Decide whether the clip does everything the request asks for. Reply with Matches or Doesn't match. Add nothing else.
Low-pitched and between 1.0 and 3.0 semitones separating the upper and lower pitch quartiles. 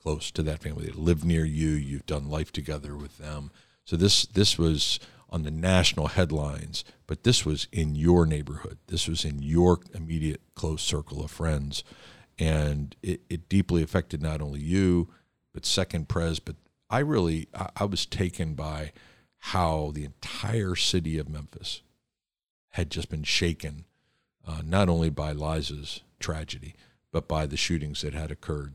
Matches